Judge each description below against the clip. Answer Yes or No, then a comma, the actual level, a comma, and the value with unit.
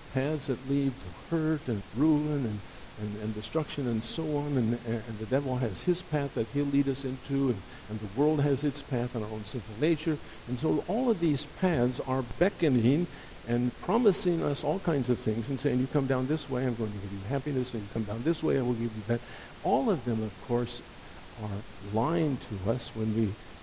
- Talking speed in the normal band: No, fast, 225 wpm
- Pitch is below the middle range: Yes, low, 130 Hz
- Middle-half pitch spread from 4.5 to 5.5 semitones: Yes, average, 4.8 semitones